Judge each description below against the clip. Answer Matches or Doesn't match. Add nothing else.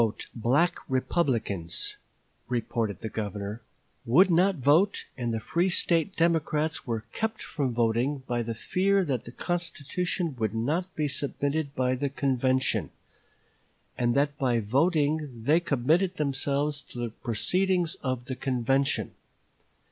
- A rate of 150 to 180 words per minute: Doesn't match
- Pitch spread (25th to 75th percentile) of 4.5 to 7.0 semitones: Matches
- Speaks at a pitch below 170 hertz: Matches